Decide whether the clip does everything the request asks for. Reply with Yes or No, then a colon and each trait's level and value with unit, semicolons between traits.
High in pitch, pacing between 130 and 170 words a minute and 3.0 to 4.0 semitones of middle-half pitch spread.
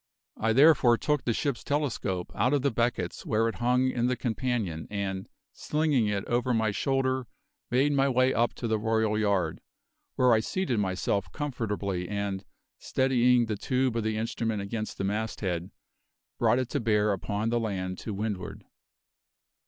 No: low, 115 Hz; average, 165 wpm; average, 3.7 semitones